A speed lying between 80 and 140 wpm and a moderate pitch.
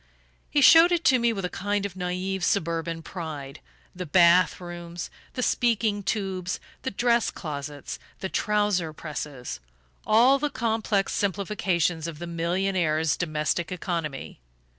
Yes: slow, 135 wpm; medium, 180 Hz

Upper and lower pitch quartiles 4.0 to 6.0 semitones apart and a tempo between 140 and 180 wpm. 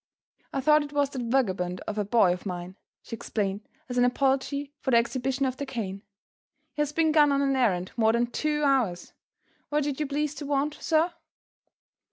No: average, 4.7 semitones; average, 200 wpm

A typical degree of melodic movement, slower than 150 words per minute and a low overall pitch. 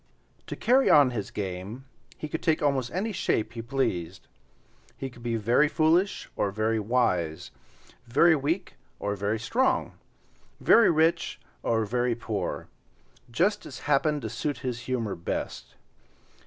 No: wide, 6.1 semitones; average, 140 wpm; low, 125 Hz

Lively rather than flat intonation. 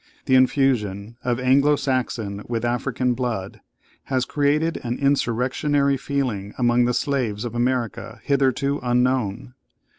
No: average, 2.7 semitones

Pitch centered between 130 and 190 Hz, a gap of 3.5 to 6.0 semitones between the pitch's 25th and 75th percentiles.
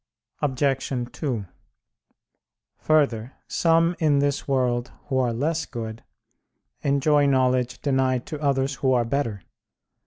No: low, 135 Hz; narrow, 2.6 semitones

